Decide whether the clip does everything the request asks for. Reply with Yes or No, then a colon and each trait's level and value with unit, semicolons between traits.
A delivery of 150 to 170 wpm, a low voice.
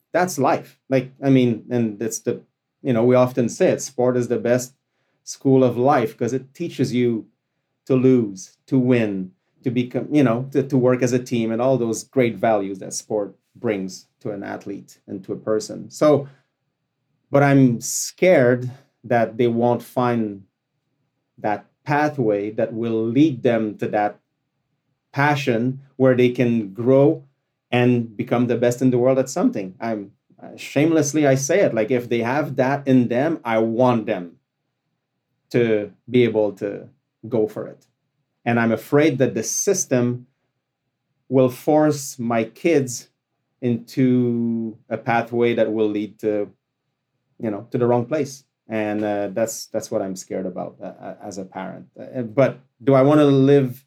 Yes: average, 165 wpm; low, 125 Hz